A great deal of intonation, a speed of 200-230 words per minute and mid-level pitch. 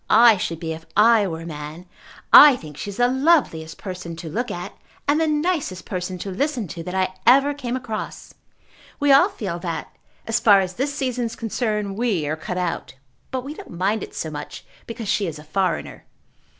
No: wide, 6.4 semitones; fast, 205 wpm; high, 205 Hz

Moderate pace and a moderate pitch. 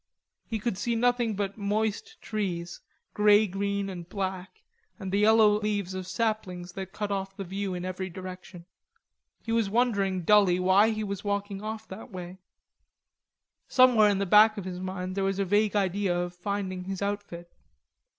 No: average, 170 wpm; high, 200 Hz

